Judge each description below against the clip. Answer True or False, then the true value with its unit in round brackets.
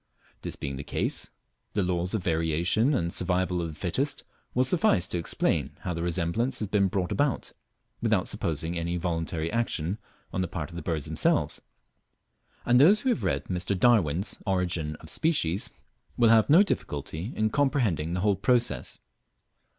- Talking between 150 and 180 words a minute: True (165 wpm)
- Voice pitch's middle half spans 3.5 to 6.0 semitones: True (5.5 semitones)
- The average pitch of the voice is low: True (90 Hz)